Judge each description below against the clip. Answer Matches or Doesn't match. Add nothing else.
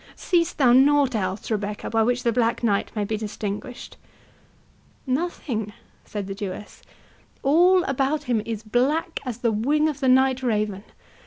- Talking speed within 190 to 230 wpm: Doesn't match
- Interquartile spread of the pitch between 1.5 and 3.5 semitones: Doesn't match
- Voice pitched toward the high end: Matches